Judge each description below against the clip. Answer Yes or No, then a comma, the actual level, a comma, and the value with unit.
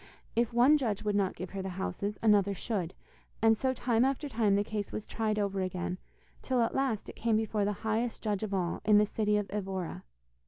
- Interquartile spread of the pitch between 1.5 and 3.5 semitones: Yes, narrow, 2.4 semitones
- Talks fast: Yes, fast, 220 wpm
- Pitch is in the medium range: No, high, 210 Hz